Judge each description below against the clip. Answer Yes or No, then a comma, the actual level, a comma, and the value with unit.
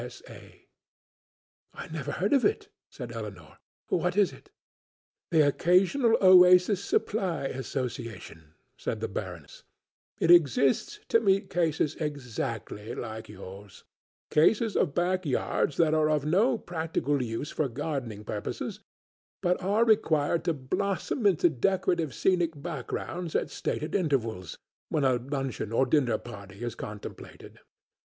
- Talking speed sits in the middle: No, slow, 125 wpm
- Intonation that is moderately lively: No, wide, 7.1 semitones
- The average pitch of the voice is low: No, medium, 150 Hz